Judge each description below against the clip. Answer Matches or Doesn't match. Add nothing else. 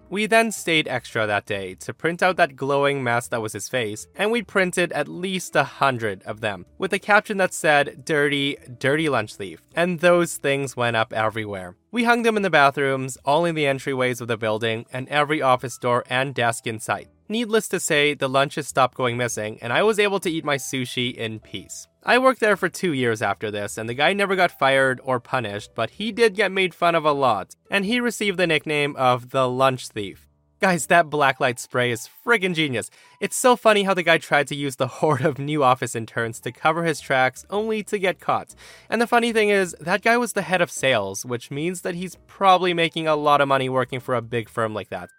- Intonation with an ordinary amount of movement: Doesn't match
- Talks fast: Matches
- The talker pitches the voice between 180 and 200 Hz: Doesn't match